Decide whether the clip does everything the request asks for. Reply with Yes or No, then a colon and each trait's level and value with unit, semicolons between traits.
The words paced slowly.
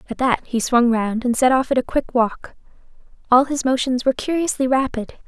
No: fast, 205 wpm